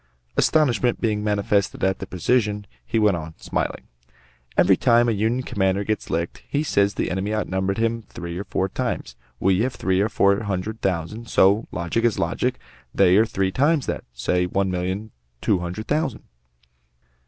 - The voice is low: Yes, low, 100 Hz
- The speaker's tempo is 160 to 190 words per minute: Yes, average, 170 wpm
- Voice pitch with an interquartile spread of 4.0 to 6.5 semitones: No, average, 3.3 semitones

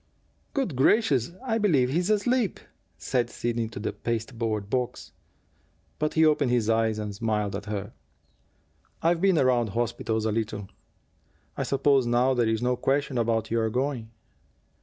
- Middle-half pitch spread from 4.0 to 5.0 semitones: Yes, average, 4.3 semitones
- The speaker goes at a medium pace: Yes, average, 150 wpm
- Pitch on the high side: No, low, 120 Hz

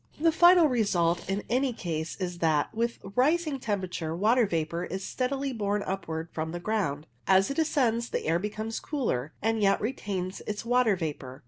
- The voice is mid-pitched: No, high, 205 Hz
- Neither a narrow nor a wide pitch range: No, wide, 6.3 semitones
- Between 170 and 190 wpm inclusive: Yes, average, 175 wpm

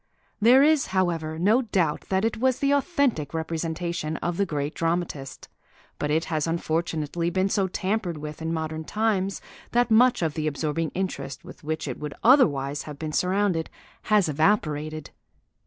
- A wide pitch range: No, average, 4.6 semitones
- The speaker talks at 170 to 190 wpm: No, average, 160 wpm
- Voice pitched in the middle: Yes, medium, 165 Hz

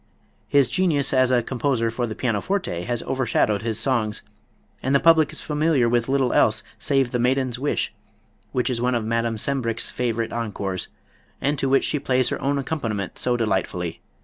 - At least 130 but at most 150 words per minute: No, average, 175 wpm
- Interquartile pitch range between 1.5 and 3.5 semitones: Yes, average, 3.1 semitones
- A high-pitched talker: No, low, 125 Hz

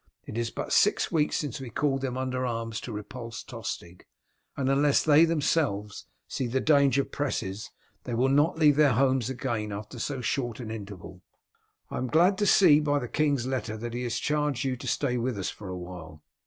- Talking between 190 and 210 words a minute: Yes, average, 200 wpm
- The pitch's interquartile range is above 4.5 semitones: No, average, 4.1 semitones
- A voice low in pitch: Yes, low, 130 Hz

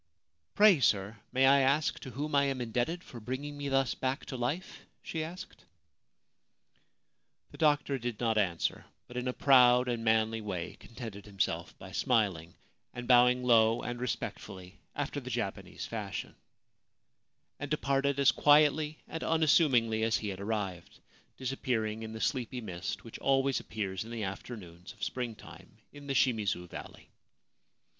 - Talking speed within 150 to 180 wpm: Yes, average, 155 wpm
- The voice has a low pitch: Yes, low, 120 Hz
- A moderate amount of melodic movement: Yes, average, 4.2 semitones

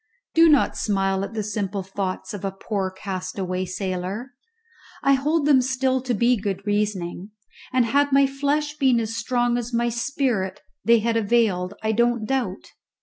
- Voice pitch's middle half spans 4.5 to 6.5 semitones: Yes, average, 4.9 semitones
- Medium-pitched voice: No, high, 225 Hz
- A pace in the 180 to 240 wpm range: No, average, 165 wpm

